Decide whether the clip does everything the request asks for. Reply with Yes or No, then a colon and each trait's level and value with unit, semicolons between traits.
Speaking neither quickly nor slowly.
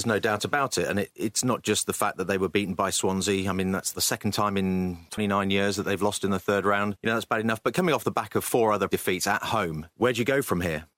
No: fast, 305 wpm